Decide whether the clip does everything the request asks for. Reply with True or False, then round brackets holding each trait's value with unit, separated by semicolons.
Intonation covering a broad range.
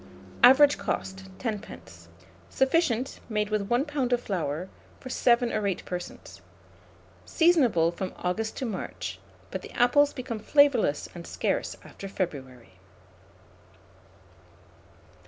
True (6.3 semitones)